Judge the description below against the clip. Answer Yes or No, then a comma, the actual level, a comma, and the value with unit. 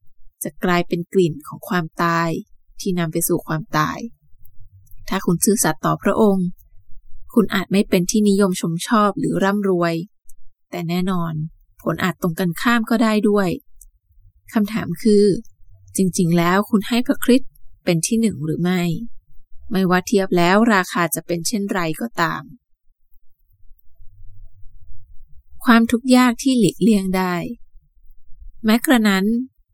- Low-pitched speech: No, medium, 180 Hz